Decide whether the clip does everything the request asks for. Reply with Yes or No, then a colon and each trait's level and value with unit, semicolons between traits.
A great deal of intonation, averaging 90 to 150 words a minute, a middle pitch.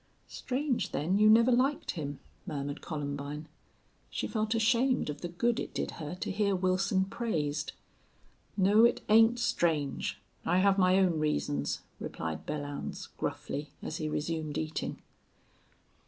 Yes: wide, 6.6 semitones; average, 140 wpm; medium, 180 Hz